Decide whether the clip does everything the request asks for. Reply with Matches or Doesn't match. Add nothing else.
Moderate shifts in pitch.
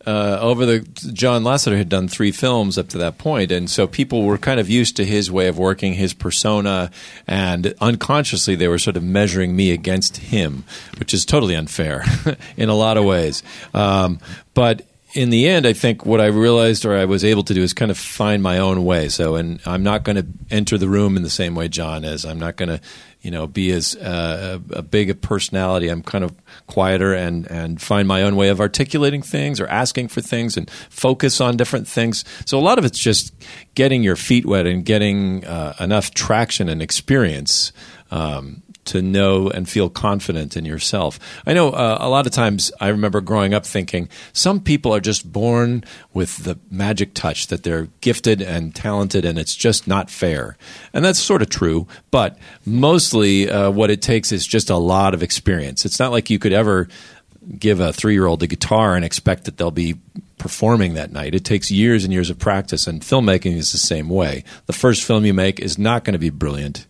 Matches